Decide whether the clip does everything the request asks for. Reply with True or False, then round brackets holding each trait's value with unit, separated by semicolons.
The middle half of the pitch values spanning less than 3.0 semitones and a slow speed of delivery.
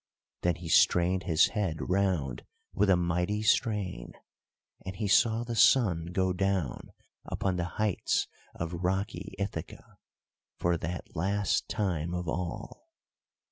True (2.6 semitones; 130 wpm)